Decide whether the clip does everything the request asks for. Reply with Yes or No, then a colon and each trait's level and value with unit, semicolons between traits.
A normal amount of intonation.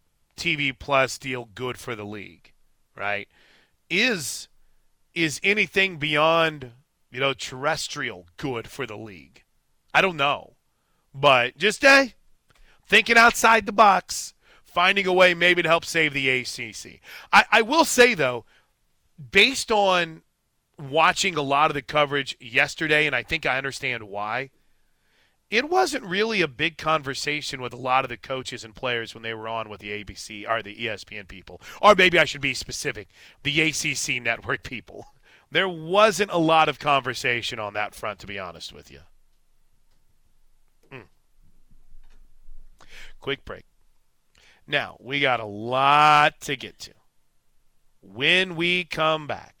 No: wide, 6.3 semitones